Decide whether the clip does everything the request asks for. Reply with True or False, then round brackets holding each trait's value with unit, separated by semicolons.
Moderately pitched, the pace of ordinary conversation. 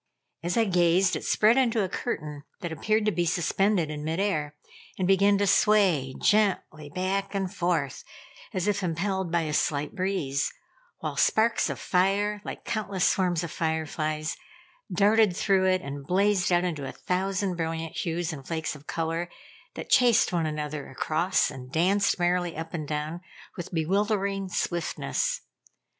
True (180 Hz; 160 wpm)